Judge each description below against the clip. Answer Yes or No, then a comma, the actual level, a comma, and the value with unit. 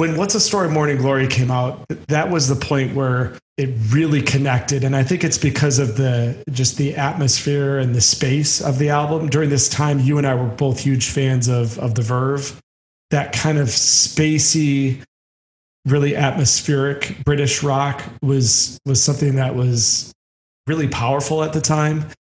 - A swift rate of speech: No, average, 175 wpm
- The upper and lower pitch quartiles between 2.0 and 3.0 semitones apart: Yes, narrow, 2.5 semitones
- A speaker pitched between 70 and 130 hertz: No, medium, 140 Hz